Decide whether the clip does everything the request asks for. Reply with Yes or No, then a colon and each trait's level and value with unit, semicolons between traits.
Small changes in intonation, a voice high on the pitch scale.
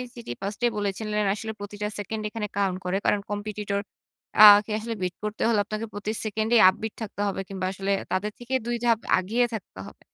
Yes: narrow, 1.7 semitones; high, 210 Hz